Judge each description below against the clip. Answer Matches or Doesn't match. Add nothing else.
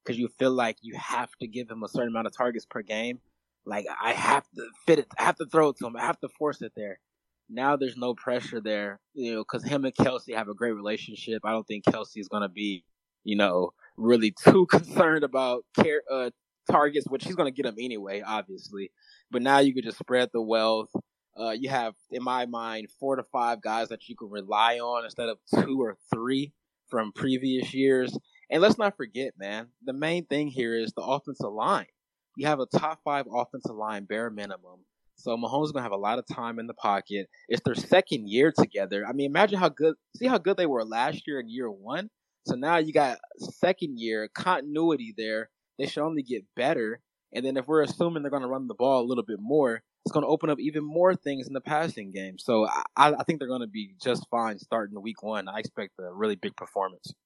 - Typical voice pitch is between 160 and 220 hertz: Doesn't match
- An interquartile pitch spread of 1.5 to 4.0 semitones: Doesn't match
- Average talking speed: Doesn't match